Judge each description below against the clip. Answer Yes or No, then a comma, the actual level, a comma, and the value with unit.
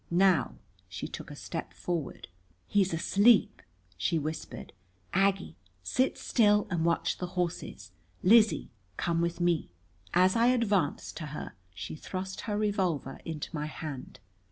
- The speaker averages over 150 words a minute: No, slow, 135 wpm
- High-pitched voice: No, medium, 175 Hz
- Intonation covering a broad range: No, average, 4.4 semitones